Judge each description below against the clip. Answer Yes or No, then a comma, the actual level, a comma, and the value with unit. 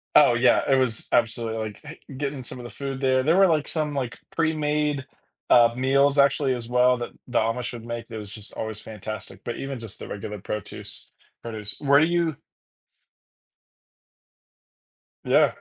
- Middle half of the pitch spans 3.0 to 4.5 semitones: Yes, average, 3.9 semitones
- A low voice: Yes, low, 125 Hz